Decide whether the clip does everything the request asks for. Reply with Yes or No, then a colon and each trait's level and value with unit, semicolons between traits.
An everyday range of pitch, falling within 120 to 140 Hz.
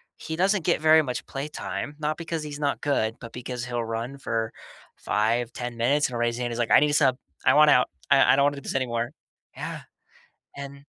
Yes: average, 3.7 semitones; low, 135 Hz